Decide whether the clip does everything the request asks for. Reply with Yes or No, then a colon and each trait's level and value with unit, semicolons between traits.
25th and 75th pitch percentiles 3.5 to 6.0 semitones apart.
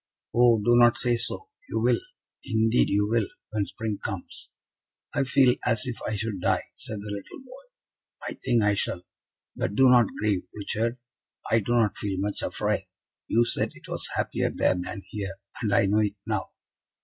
No: average, 2.8 semitones